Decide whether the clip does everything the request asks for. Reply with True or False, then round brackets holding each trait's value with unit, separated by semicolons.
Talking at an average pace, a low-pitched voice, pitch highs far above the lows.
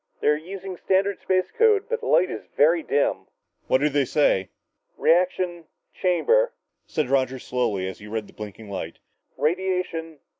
False (175 wpm; 165 Hz; 6.3 semitones)